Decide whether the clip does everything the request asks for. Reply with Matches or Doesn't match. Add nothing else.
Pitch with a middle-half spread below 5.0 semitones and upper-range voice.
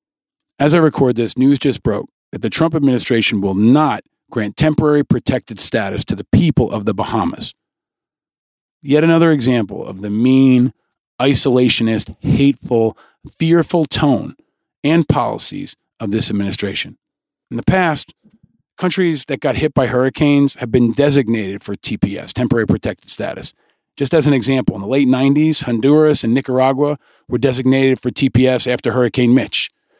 Doesn't match